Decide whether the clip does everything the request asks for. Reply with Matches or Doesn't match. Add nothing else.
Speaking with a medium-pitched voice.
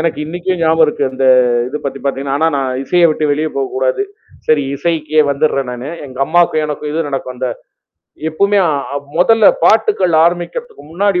Matches